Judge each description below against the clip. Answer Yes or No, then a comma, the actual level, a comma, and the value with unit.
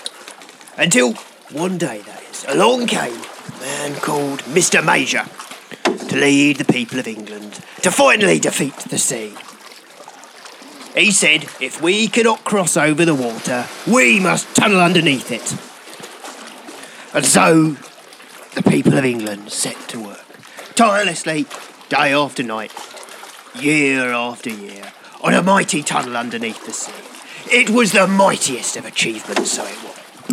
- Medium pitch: Yes, medium, 145 Hz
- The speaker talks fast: No, slow, 135 wpm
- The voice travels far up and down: Yes, wide, 7.1 semitones